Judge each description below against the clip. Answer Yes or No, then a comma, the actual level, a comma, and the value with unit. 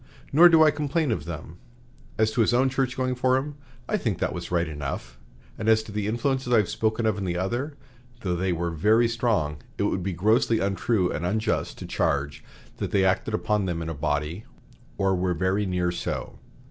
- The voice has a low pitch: Yes, low, 105 Hz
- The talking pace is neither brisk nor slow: No, fast, 210 wpm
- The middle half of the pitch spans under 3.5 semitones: No, average, 5.3 semitones